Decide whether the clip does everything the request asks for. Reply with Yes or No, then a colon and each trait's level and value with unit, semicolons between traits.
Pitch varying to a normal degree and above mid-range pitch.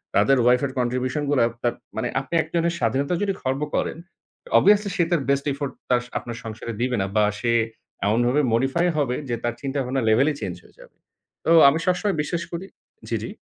No: average, 4.9 semitones; low, 135 Hz